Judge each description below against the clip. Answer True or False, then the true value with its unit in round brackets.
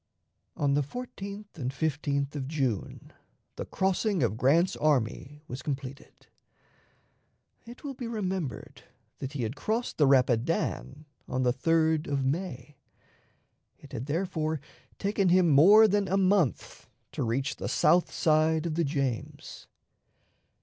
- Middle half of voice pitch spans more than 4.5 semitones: True (5.5 semitones)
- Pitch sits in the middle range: True (155 Hz)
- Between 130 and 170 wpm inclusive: True (135 wpm)